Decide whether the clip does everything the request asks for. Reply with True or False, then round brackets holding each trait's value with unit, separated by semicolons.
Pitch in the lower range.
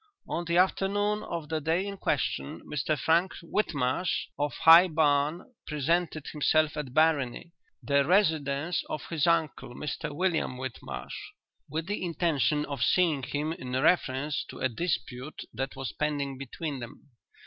False (155 Hz)